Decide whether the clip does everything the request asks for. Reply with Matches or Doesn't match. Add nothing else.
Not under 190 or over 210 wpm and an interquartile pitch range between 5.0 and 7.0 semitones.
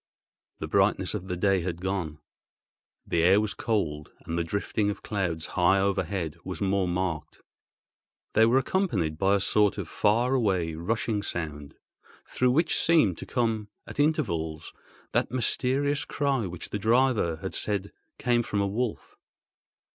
Doesn't match